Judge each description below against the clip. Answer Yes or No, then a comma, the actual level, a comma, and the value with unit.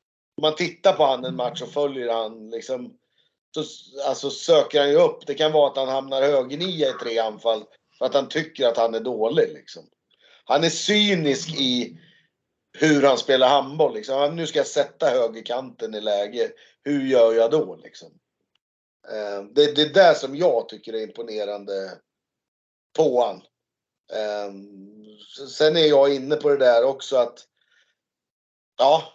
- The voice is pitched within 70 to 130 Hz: No, medium, 140 Hz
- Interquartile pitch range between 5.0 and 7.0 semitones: Yes, average, 5.3 semitones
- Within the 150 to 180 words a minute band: Yes, average, 165 wpm